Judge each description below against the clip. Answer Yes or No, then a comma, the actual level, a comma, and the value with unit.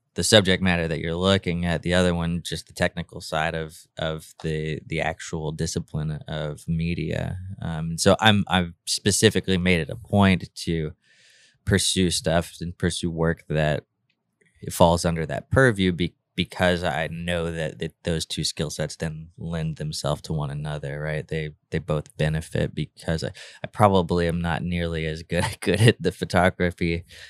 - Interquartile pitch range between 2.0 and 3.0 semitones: Yes, narrow, 2.5 semitones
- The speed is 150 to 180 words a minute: Yes, average, 165 wpm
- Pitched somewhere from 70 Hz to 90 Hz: Yes, very low, 85 Hz